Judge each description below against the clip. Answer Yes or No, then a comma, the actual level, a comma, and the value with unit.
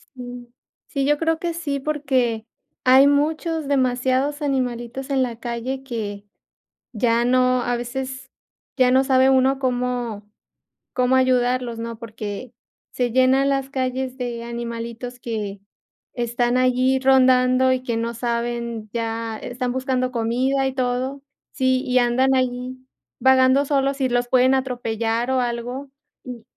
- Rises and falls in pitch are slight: Yes, narrow, 1.9 semitones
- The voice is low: No, very high, 255 Hz